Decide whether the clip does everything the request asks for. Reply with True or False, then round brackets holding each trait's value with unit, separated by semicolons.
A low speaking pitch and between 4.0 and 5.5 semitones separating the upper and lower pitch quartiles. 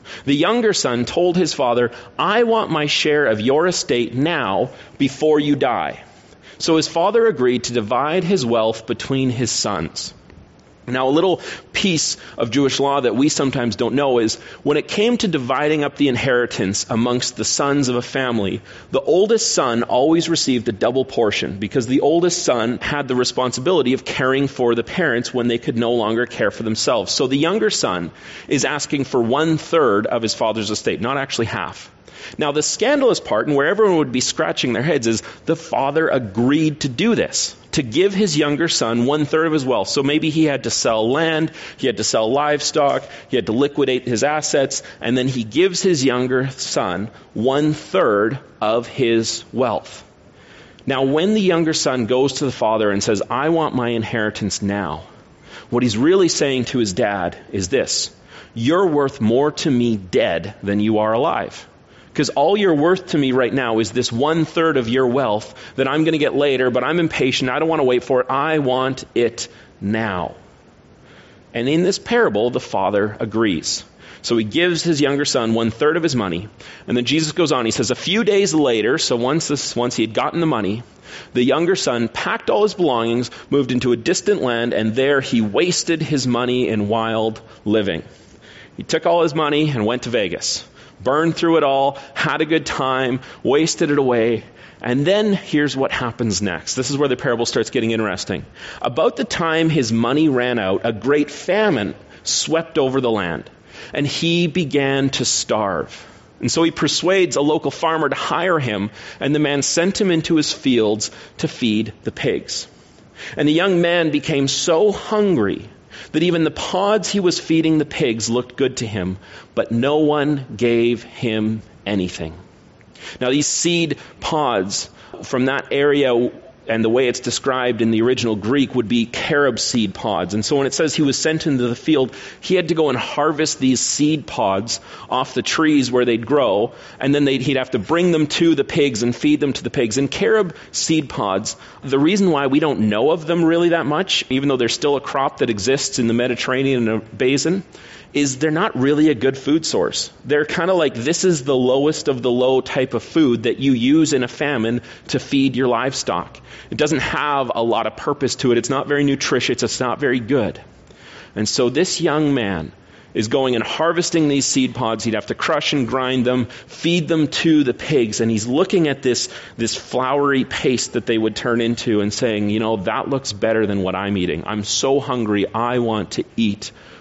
True (130 Hz; 4.8 semitones)